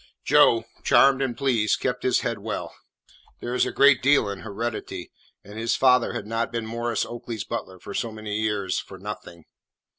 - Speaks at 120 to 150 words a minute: No, average, 180 wpm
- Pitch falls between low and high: No, low, 115 Hz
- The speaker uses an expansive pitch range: No, narrow, 2.5 semitones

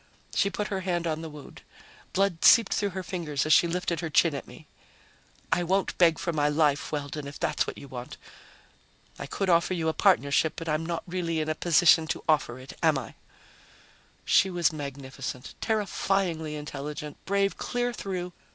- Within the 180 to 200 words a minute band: Yes, average, 185 wpm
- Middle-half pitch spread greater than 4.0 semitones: No, average, 3.6 semitones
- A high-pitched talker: No, medium, 165 Hz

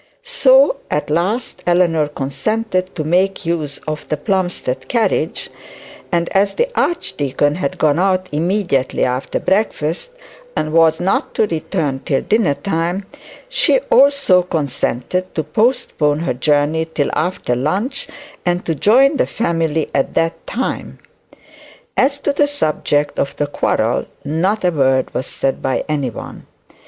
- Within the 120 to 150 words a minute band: Yes, average, 140 wpm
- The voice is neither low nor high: Yes, medium, 170 Hz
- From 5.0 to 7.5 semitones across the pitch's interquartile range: Yes, wide, 5.4 semitones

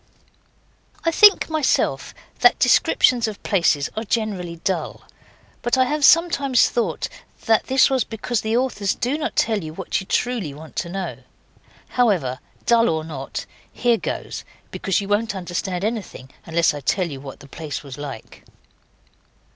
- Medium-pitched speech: No, high, 205 Hz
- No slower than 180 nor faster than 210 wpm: No, average, 155 wpm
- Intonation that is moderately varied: No, wide, 6.9 semitones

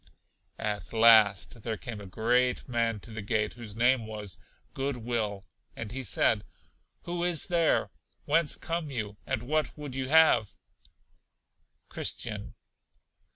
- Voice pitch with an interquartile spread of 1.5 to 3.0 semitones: No, average, 4.1 semitones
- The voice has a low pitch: Yes, low, 115 Hz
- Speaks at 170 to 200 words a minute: No, slow, 135 wpm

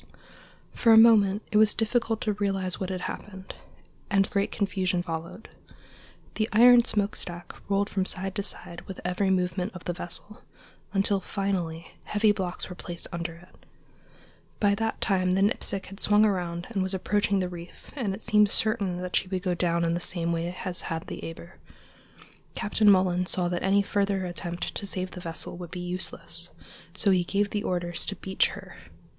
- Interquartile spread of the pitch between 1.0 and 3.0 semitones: Yes, narrow, 2.5 semitones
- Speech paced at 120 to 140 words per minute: No, average, 185 wpm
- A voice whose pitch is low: No, high, 190 Hz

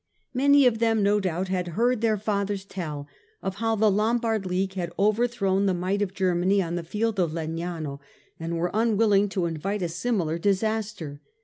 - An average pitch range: Yes, average, 3.9 semitones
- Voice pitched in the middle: No, high, 195 Hz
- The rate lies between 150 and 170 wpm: No, average, 185 wpm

